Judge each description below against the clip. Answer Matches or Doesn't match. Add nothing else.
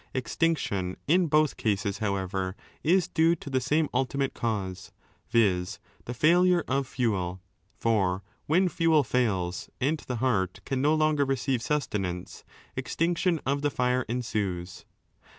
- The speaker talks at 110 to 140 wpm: Matches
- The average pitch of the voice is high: Doesn't match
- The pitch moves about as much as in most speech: Doesn't match